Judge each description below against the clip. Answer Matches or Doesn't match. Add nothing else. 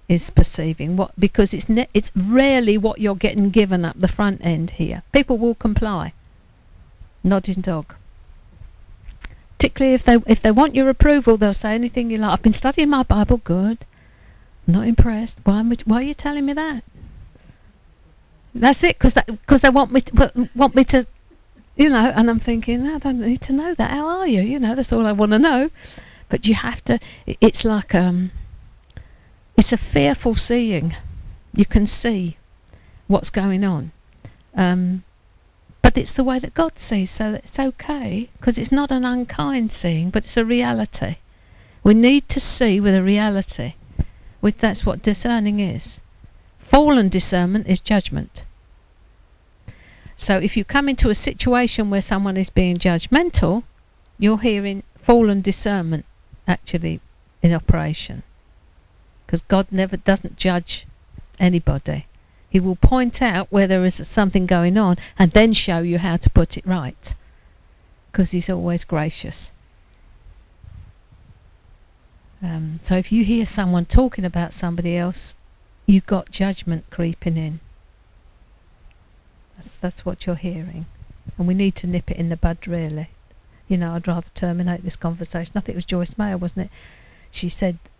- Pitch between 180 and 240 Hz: Matches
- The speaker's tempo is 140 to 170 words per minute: Matches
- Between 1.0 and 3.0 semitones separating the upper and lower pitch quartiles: Doesn't match